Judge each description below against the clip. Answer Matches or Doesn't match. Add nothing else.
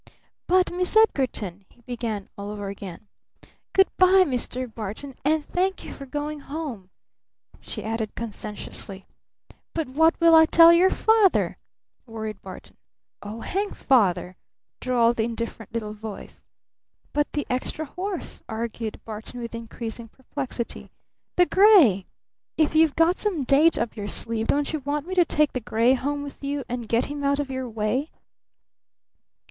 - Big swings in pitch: Matches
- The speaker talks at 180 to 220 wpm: Doesn't match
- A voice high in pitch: Matches